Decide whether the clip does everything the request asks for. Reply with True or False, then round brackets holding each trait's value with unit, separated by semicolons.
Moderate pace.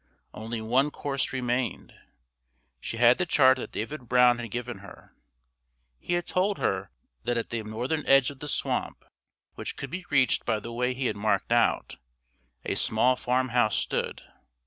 True (170 wpm)